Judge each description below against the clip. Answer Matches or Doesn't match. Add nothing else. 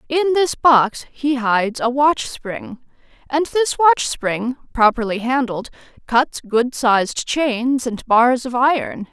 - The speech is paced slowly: Doesn't match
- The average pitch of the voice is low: Doesn't match